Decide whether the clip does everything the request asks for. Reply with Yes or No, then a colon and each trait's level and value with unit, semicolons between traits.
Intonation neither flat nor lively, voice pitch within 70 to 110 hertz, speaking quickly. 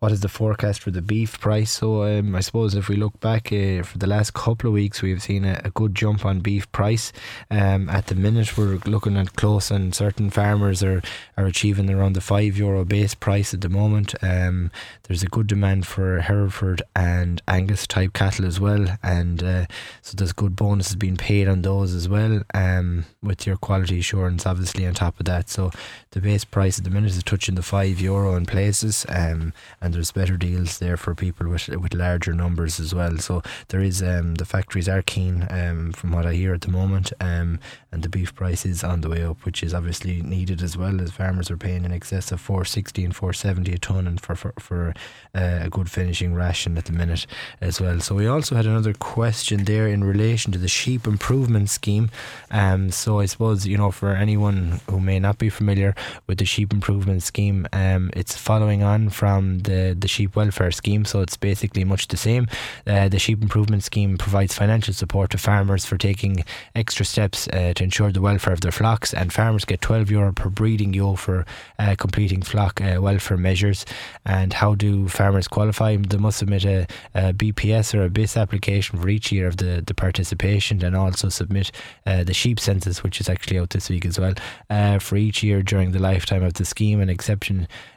No: narrow, 2.1 semitones; low, 100 Hz; fast, 210 wpm